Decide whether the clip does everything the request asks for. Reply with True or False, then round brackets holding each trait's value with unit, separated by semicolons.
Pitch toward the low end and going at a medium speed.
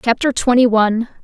False (240 Hz; 145 wpm)